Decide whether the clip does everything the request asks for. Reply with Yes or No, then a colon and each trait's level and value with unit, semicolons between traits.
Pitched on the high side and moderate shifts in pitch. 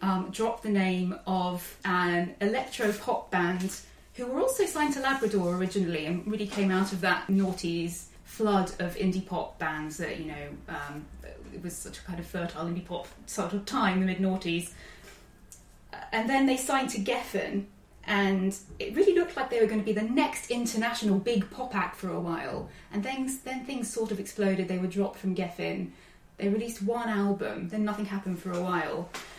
Yes: high, 195 Hz; average, 3.8 semitones